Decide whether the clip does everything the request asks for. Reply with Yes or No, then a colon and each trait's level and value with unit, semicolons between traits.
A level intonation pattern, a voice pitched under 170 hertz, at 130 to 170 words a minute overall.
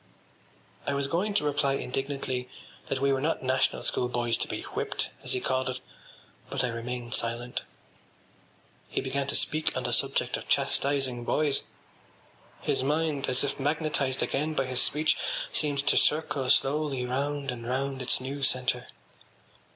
Yes: narrow, 2.2 semitones; low, 135 Hz; average, 160 wpm